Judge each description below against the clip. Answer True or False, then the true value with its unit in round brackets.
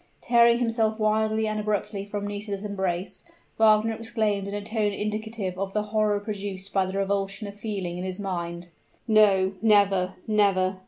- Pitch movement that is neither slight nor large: False (1.8 semitones)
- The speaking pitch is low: False (205 Hz)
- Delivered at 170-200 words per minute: False (160 wpm)